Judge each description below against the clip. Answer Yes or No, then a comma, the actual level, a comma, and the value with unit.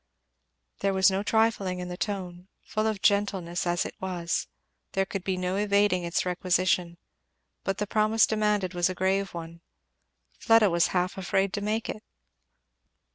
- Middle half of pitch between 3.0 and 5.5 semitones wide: No, narrow, 2.4 semitones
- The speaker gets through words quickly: No, average, 160 wpm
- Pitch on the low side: No, high, 190 Hz